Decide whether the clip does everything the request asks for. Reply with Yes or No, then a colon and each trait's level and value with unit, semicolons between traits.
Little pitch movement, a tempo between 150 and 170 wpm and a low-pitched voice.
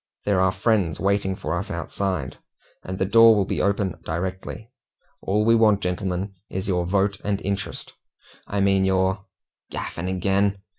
Yes: narrow, 1.4 semitones; average, 160 wpm; very low, 95 Hz